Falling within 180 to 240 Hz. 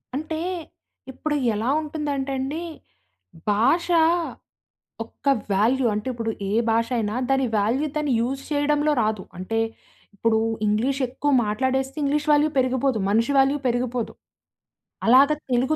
No: very high, 260 Hz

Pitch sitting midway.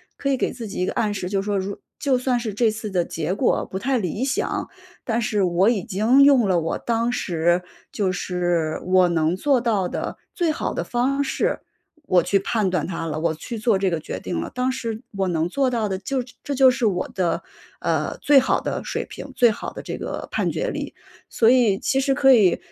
No: high, 210 Hz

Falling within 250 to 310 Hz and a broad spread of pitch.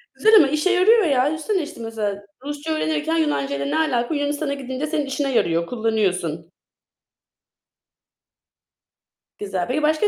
Yes: very high, 285 Hz; wide, 6.4 semitones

